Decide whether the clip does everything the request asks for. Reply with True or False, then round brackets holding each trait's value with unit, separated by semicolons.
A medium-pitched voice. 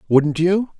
True (170 Hz)